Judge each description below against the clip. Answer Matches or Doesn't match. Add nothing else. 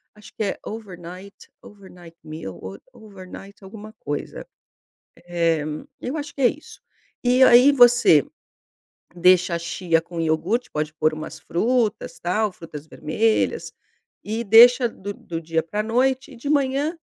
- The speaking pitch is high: Matches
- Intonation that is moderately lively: Doesn't match